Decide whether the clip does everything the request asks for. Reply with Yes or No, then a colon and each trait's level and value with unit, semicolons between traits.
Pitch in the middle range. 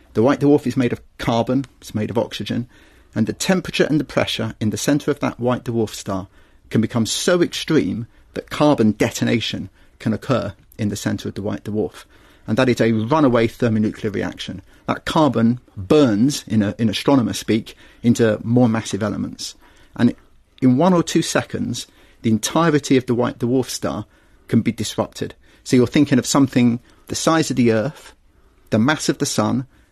No: low, 120 Hz